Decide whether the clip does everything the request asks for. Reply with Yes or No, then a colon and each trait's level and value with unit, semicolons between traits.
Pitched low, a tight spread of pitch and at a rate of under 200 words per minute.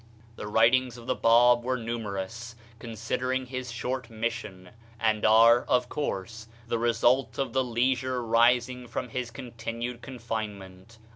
Yes: low, 120 Hz; narrow, 1.8 semitones; slow, 135 wpm